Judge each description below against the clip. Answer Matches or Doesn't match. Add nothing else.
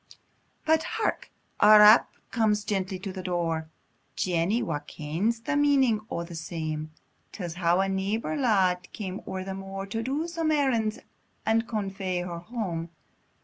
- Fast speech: Doesn't match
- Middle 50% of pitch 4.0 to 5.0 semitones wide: Matches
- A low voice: Doesn't match